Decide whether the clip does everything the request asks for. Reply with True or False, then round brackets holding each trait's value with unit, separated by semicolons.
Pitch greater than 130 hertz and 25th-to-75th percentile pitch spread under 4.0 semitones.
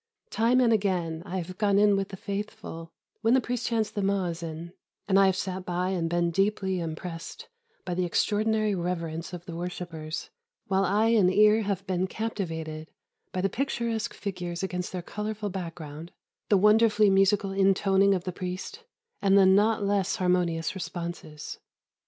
True (190 Hz; 3.0 semitones)